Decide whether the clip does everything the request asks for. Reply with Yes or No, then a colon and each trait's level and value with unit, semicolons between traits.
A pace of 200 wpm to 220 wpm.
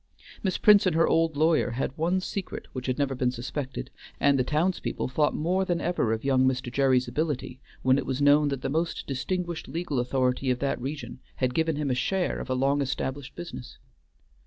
Yes: fast, 205 wpm